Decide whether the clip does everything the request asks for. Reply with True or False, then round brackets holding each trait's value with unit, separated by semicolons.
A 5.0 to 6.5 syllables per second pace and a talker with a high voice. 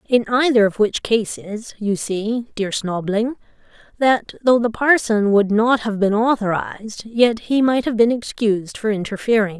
False (4.5 syllables/s; 220 Hz)